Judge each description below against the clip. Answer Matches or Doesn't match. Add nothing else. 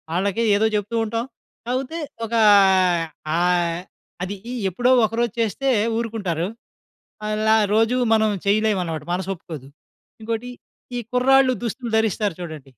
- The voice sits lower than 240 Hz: Matches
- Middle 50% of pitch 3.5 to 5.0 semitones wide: Matches